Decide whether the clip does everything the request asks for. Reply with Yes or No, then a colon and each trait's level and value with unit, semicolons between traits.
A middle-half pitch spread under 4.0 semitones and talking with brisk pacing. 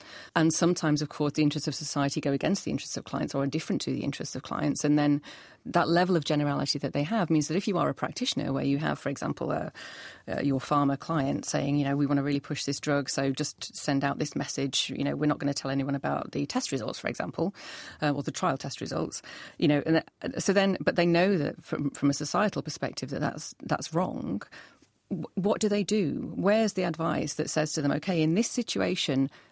Yes: average, 3.4 semitones; fast, 240 wpm